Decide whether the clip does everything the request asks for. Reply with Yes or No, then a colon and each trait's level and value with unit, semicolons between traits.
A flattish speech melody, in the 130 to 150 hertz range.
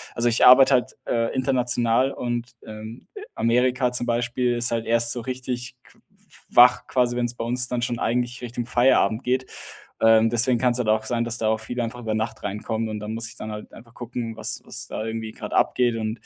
No: narrow, 1.6 semitones; low, 120 Hz